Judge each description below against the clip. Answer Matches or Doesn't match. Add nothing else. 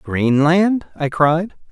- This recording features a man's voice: Matches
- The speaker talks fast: Doesn't match